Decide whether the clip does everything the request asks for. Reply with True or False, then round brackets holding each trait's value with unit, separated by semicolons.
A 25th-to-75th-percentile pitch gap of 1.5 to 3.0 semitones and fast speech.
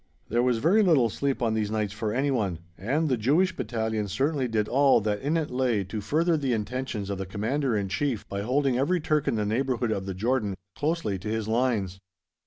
False (4.8 semitones; 210 wpm)